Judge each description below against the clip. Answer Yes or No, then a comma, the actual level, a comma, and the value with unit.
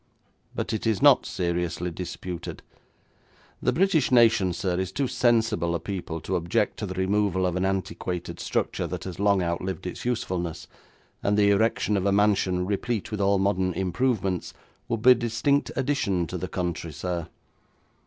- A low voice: Yes, very low, 95 Hz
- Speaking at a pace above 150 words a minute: Yes, average, 165 wpm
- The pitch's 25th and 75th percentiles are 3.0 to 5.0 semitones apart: Yes, average, 3.9 semitones